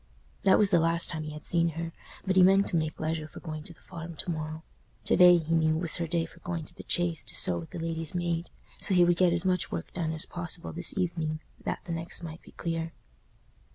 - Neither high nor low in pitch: Yes, medium, 165 Hz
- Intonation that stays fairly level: Yes, narrow, 1.6 semitones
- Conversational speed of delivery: No, fast, 255 wpm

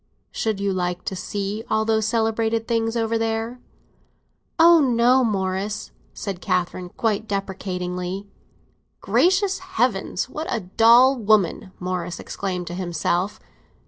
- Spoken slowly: Yes, slow, 120 wpm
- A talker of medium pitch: No, high, 210 Hz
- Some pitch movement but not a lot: Yes, average, 3.5 semitones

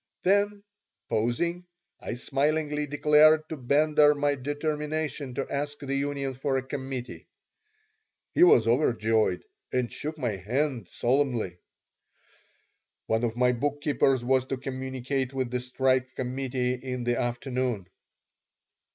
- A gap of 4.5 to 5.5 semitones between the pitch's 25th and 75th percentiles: No, average, 2.9 semitones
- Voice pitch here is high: No, low, 135 Hz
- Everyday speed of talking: No, slow, 120 wpm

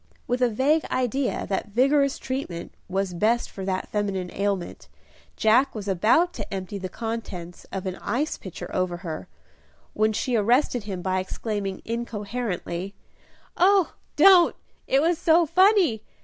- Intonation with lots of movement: Yes, wide, 5.8 semitones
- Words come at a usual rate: Yes, average, 145 wpm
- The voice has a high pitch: Yes, high, 215 Hz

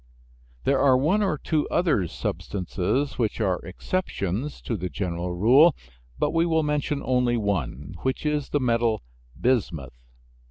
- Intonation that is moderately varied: No, wide, 8.0 semitones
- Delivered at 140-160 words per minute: Yes, average, 145 wpm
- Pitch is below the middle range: Yes, low, 125 Hz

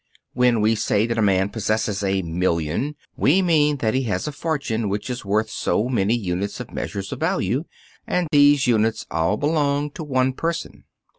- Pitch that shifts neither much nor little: No, wide, 6.0 semitones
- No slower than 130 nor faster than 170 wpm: No, average, 180 wpm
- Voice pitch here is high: No, low, 115 Hz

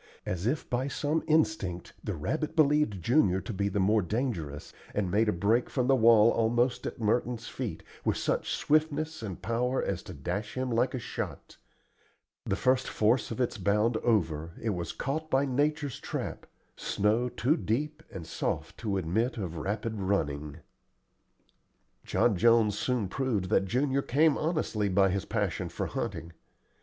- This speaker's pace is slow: No, average, 165 wpm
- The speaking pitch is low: Yes, low, 115 Hz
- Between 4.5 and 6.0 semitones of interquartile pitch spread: Yes, average, 5.2 semitones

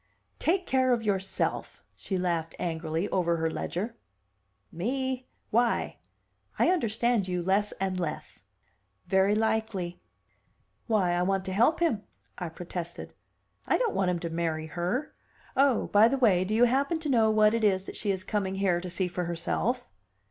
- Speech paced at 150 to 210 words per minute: Yes, average, 165 wpm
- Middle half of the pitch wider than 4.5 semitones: Yes, average, 4.9 semitones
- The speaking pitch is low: No, high, 195 Hz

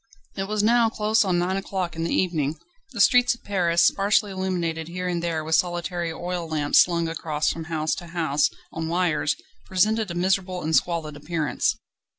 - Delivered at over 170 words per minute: Yes, average, 180 wpm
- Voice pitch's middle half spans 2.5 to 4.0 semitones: Yes, average, 2.8 semitones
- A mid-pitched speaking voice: Yes, medium, 175 Hz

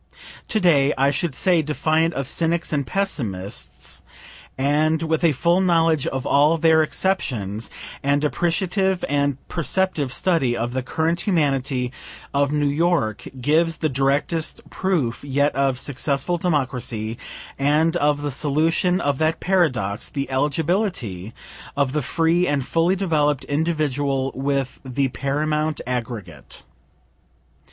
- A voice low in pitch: No, medium, 145 Hz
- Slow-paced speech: Yes, slow, 130 wpm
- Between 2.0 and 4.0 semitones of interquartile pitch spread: Yes, average, 3.6 semitones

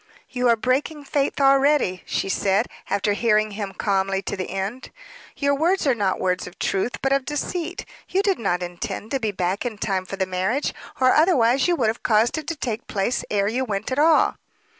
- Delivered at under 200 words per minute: No, fast, 205 wpm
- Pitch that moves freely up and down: Yes, wide, 5.9 semitones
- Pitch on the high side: Yes, high, 230 Hz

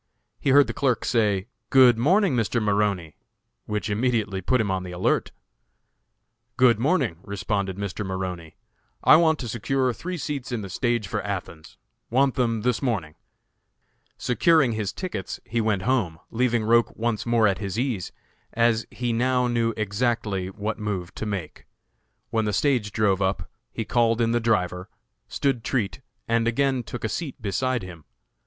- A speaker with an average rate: Yes, average, 160 wpm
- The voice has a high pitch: No, low, 115 Hz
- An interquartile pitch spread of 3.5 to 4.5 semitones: Yes, average, 3.9 semitones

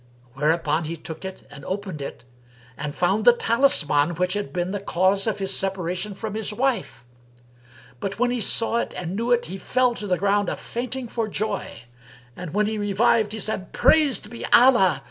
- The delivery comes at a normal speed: Yes, average, 190 wpm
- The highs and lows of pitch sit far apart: No, average, 4.0 semitones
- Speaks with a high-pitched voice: Yes, high, 200 Hz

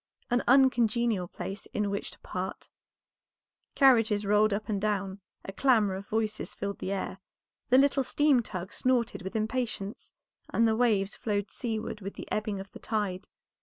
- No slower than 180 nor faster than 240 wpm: No, average, 160 wpm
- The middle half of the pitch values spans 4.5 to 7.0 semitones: No, average, 3.1 semitones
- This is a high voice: Yes, high, 215 Hz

